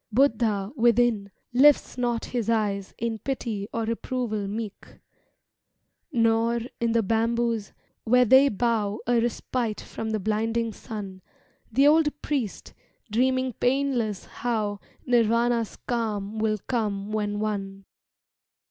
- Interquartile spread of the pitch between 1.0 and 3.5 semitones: Yes, narrow, 2.4 semitones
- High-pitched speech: Yes, high, 230 Hz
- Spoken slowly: Yes, slow, 115 wpm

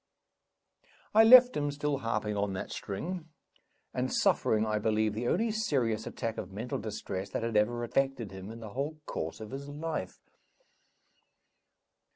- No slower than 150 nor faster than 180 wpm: Yes, average, 155 wpm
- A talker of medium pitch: No, low, 115 Hz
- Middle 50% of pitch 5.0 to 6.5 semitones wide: Yes, wide, 5.4 semitones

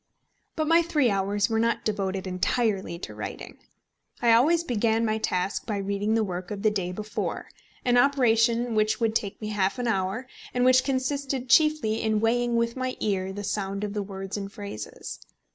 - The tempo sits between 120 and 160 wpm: No, average, 185 wpm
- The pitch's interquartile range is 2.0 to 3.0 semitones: No, average, 3.6 semitones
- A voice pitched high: Yes, high, 220 Hz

